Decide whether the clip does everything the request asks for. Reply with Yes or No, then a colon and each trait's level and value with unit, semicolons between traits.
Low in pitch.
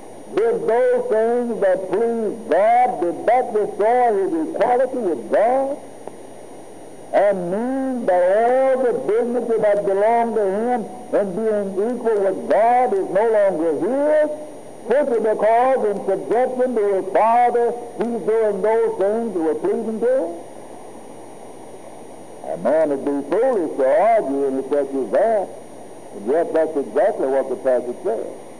No: high, 230 Hz